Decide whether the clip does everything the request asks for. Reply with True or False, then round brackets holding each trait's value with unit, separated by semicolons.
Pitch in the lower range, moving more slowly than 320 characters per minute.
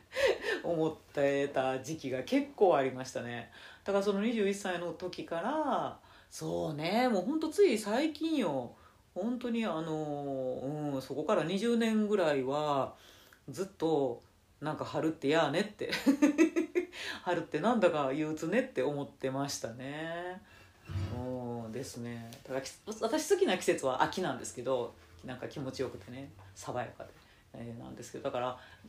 False (155 Hz; 285 characters per minute)